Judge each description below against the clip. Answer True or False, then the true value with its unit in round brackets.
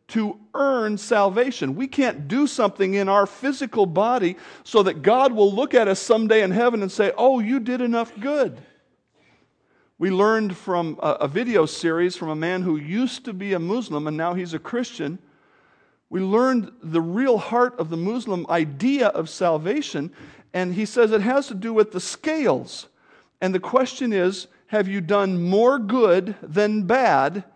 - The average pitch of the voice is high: True (205 Hz)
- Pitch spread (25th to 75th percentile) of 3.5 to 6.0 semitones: True (5.2 semitones)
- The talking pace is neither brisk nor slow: True (175 wpm)